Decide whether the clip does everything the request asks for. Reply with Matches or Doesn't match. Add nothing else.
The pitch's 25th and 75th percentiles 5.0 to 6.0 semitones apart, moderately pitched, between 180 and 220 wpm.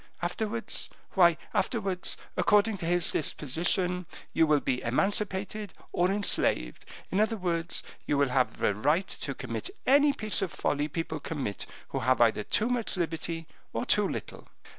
Doesn't match